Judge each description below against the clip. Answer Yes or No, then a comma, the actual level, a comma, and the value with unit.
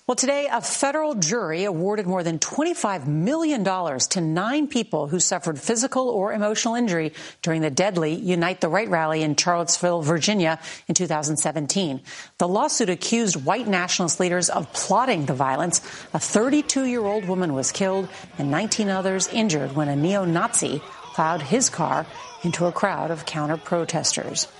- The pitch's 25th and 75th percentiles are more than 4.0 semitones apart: Yes, average, 5.1 semitones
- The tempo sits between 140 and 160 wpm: Yes, average, 150 wpm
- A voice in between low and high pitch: Yes, medium, 180 Hz